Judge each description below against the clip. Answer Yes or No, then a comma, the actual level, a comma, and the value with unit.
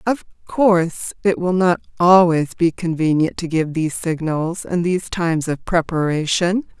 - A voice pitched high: No, medium, 170 Hz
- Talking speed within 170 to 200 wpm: No, average, 150 wpm